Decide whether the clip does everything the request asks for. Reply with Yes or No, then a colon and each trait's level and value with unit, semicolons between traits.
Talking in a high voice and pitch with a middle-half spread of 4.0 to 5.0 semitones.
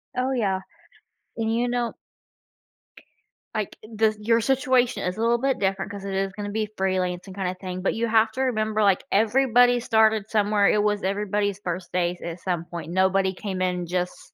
No: high, 205 Hz; average, 3.2 semitones